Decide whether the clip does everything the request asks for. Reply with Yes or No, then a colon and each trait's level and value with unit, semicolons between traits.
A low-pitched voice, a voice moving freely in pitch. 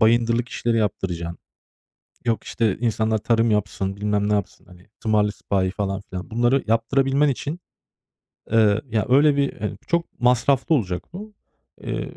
No: low, 115 Hz; average, 3.5 semitones